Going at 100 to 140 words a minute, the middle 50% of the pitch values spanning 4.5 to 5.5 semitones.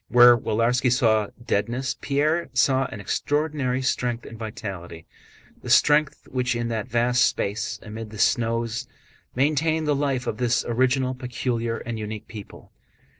No: slow, 135 wpm; average, 2.8 semitones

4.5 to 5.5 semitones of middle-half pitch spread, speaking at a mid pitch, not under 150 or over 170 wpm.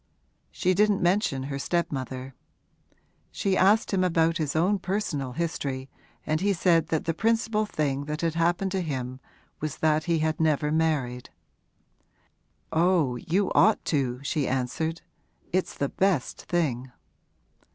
No: average, 4.8 semitones; medium, 160 Hz; average, 140 wpm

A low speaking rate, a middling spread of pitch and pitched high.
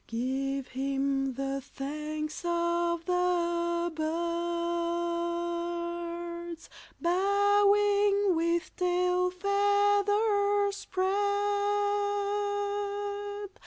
Yes: slow, 55 wpm; average, 3.1 semitones; very high, 345 Hz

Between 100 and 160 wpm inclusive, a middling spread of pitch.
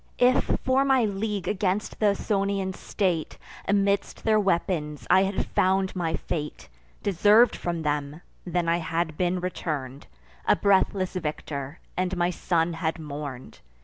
Yes: average, 140 wpm; average, 3.6 semitones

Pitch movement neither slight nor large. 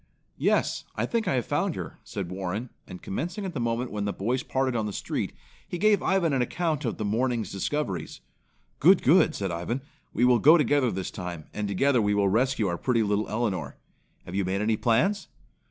No: wide, 6.0 semitones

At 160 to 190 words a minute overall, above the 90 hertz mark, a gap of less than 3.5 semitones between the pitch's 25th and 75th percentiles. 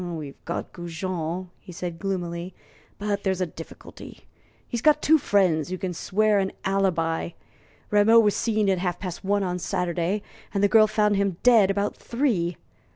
Yes: average, 170 wpm; high, 190 Hz; average, 3.1 semitones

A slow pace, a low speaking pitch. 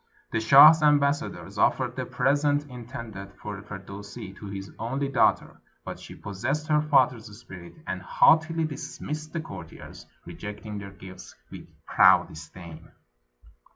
Yes: slow, 130 wpm; low, 115 Hz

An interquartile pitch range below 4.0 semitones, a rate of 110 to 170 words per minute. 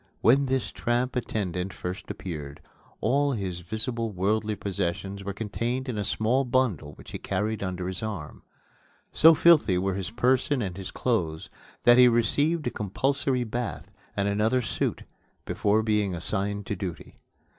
No: average, 4.5 semitones; average, 155 wpm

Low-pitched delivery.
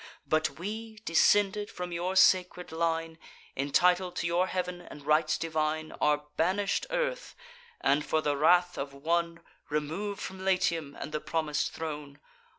No: medium, 165 Hz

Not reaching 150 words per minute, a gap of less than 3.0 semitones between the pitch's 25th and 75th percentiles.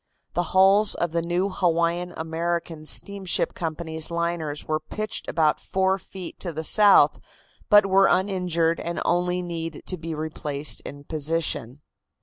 Yes: average, 140 wpm; narrow, 2.6 semitones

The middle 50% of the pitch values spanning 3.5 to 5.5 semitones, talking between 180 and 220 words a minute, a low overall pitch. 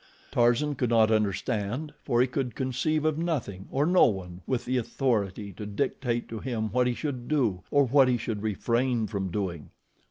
Yes: average, 4.1 semitones; average, 185 wpm; low, 120 Hz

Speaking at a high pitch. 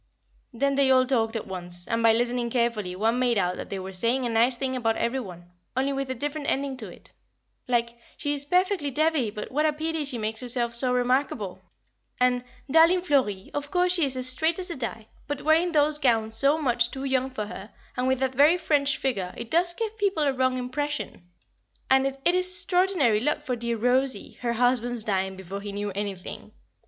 Yes: very high, 255 Hz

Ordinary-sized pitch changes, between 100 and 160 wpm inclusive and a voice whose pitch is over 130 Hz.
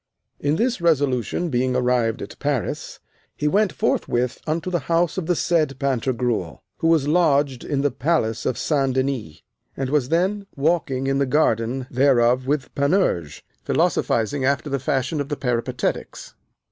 Yes: average, 3.9 semitones; average, 155 wpm; medium, 140 Hz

